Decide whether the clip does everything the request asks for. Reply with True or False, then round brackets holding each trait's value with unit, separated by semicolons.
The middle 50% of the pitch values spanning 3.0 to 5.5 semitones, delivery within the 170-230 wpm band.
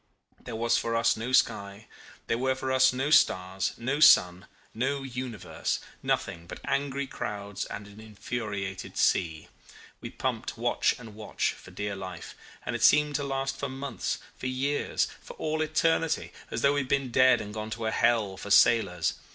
True (4.9 semitones; 175 wpm)